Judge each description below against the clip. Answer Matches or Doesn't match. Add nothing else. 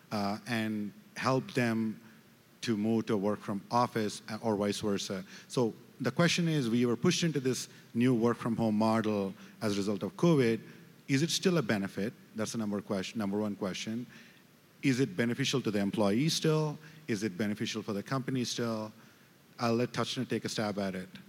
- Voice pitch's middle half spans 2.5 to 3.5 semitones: Matches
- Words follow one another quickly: Doesn't match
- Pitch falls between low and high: Doesn't match